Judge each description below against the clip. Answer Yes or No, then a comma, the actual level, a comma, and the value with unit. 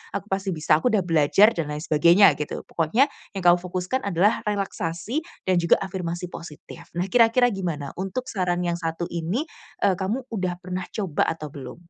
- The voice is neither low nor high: Yes, medium, 180 Hz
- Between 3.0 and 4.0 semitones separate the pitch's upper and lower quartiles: Yes, average, 3.3 semitones